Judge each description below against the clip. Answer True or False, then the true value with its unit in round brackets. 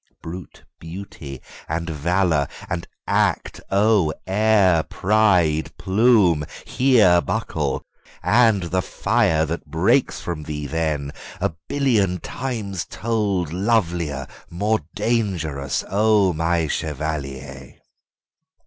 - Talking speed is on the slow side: True (90 wpm)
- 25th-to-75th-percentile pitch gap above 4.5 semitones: True (5.1 semitones)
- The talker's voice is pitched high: False (90 Hz)